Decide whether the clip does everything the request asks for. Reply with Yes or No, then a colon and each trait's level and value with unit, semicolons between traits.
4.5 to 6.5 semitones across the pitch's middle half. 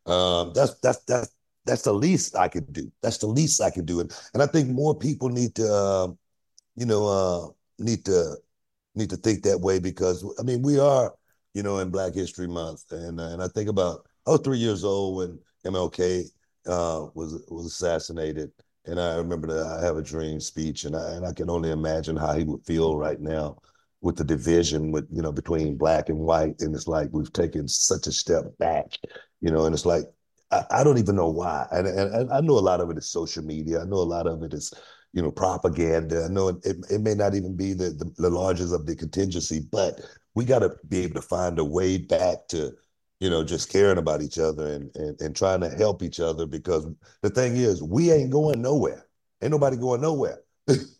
No: average, 4.0 semitones